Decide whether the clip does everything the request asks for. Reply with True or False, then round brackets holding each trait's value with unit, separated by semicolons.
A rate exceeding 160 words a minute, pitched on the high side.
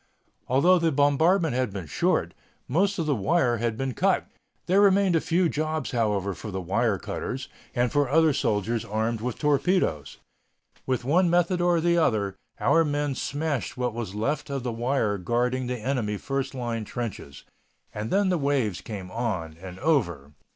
False (170 wpm; 125 Hz)